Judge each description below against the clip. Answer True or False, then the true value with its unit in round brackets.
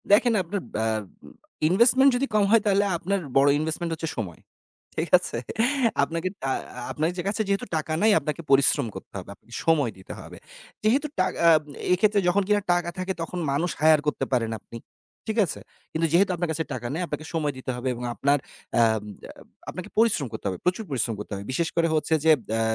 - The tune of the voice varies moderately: False (6.0 semitones)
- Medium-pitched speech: True (165 Hz)